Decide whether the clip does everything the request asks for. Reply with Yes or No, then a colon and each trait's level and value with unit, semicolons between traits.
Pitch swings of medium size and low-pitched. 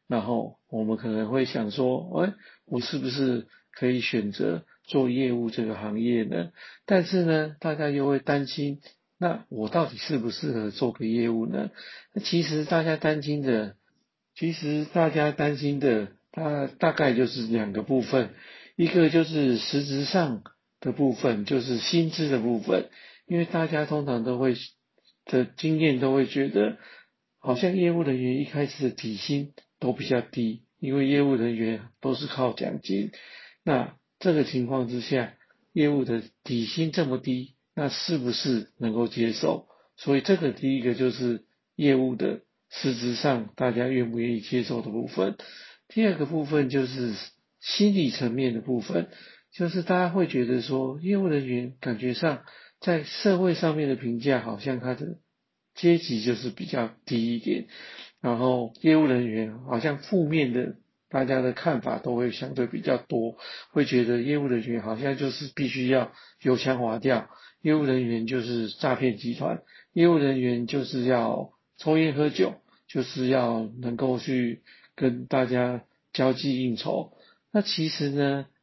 Yes: average, 3.8 semitones; low, 130 Hz